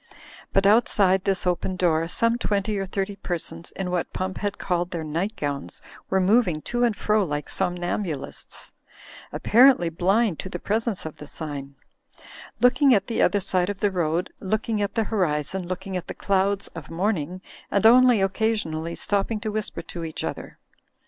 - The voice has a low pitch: No, high, 190 Hz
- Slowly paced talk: No, average, 170 wpm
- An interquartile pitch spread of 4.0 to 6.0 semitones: No, average, 3.5 semitones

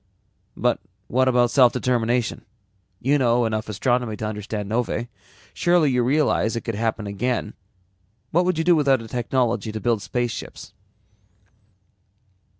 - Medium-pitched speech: No, low, 120 Hz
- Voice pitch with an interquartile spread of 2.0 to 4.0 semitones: Yes, average, 2.7 semitones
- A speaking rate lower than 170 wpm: Yes, average, 140 wpm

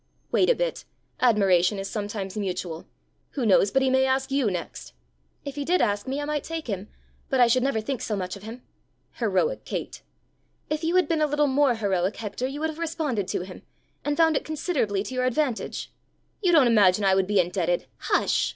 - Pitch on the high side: Yes, high, 245 Hz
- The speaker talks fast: Yes, fast, 215 wpm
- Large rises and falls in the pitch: Yes, wide, 6.8 semitones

